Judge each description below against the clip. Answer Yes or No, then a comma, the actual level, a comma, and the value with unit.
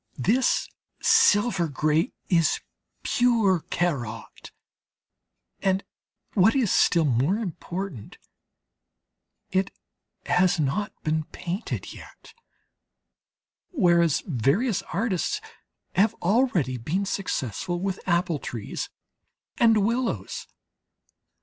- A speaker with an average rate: No, slow, 85 wpm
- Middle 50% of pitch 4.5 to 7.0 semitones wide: Yes, average, 4.9 semitones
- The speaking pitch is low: No, medium, 180 Hz